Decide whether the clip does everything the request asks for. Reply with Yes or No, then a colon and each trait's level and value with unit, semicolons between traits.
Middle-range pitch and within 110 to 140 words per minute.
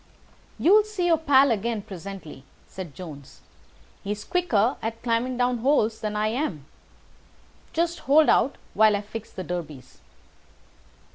No: high, 225 Hz; slow, 135 wpm